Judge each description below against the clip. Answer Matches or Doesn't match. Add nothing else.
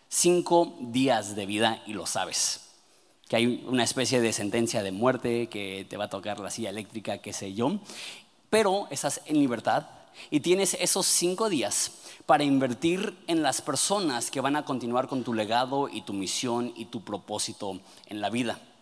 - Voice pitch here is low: Matches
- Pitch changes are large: Matches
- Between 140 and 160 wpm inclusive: Doesn't match